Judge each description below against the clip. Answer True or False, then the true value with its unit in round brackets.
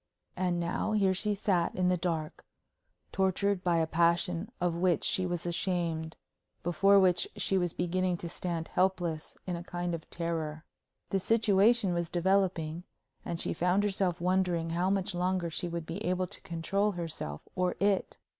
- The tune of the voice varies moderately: False (2.0 semitones)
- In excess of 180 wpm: False (165 wpm)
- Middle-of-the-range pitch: True (175 Hz)